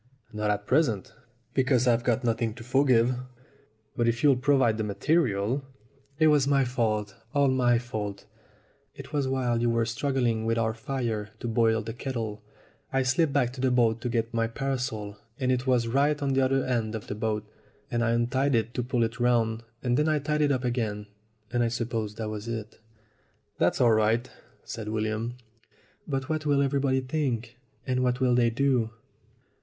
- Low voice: Yes, low, 120 Hz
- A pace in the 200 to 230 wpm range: No, average, 190 wpm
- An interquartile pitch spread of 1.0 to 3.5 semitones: Yes, average, 2.9 semitones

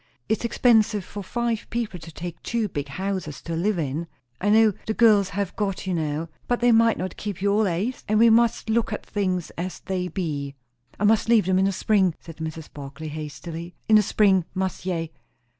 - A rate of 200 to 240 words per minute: Yes, fast, 205 wpm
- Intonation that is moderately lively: Yes, average, 4.5 semitones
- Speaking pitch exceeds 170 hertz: Yes, high, 190 Hz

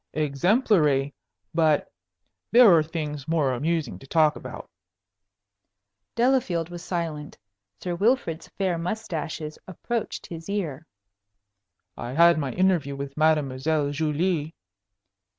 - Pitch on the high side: No, medium, 160 Hz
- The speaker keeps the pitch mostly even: No, average, 3.2 semitones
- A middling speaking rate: No, slow, 105 wpm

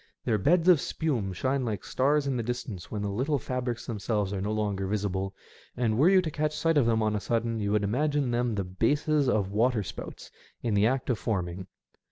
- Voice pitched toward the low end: Yes, low, 115 Hz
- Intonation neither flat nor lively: Yes, average, 4.8 semitones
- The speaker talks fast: Yes, fast, 220 wpm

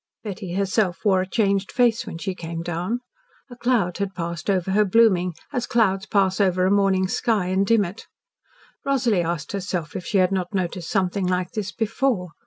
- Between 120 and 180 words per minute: No, average, 190 wpm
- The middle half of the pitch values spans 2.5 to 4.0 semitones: Yes, average, 2.8 semitones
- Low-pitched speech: No, high, 190 Hz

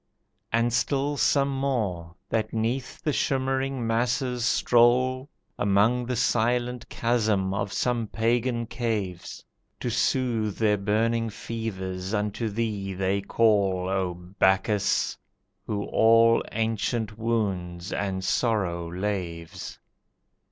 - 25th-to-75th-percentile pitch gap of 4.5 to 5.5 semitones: No, average, 3.7 semitones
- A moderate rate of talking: No, slow, 105 wpm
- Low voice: Yes, low, 110 Hz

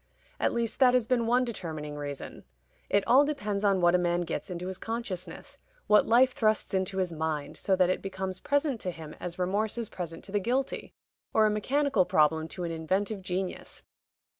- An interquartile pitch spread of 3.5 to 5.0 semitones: Yes, average, 4.7 semitones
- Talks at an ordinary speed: Yes, average, 195 wpm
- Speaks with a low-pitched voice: No, high, 190 Hz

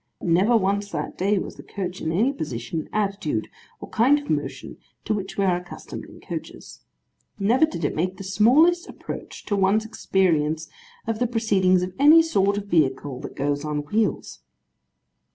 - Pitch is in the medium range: No, high, 195 Hz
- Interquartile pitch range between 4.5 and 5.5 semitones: Yes, average, 4.9 semitones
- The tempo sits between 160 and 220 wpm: Yes, average, 175 wpm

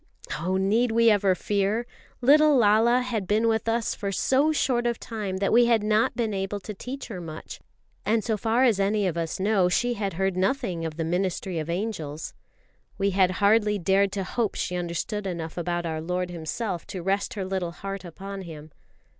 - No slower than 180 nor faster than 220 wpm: Yes, average, 195 wpm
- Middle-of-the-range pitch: No, high, 195 Hz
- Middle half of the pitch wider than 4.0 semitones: No, average, 3.7 semitones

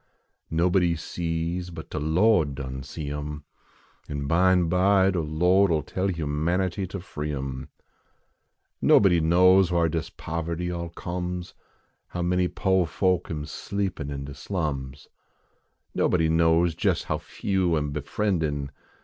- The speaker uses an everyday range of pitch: Yes, average, 3.3 semitones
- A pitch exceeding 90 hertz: No, very low, 85 Hz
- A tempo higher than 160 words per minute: No, average, 140 wpm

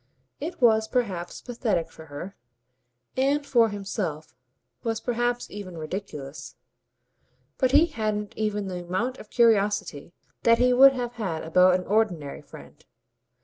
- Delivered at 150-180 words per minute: No, slow, 135 wpm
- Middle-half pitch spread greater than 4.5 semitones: Yes, wide, 5.4 semitones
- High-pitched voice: Yes, high, 210 Hz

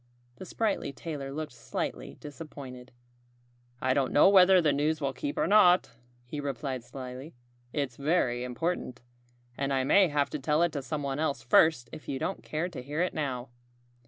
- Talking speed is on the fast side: No, average, 175 wpm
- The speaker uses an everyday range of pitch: Yes, average, 3.7 semitones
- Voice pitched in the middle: Yes, medium, 145 Hz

